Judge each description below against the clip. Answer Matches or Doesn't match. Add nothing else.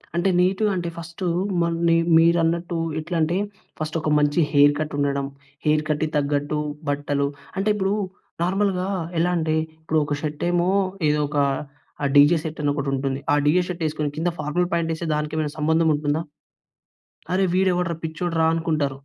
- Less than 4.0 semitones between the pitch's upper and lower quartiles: Matches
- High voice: Doesn't match